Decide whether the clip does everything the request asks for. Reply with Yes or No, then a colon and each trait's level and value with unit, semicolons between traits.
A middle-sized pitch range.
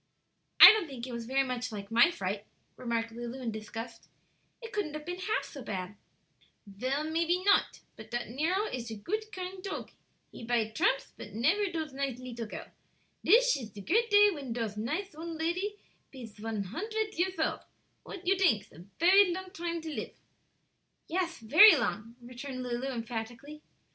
No: wide, 7.9 semitones